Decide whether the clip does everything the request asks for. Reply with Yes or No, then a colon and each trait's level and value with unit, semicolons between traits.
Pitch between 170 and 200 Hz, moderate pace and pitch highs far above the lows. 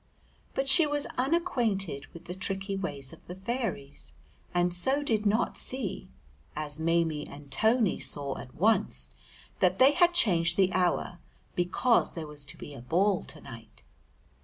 Yes: medium, 185 Hz; average, 160 wpm; wide, 7.3 semitones